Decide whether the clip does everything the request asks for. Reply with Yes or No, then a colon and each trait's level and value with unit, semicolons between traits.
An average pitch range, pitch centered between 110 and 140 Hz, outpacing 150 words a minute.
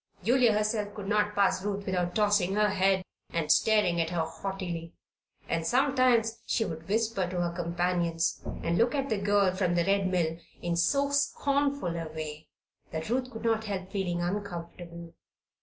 No: average, 4.0 semitones; high, 190 Hz; average, 170 wpm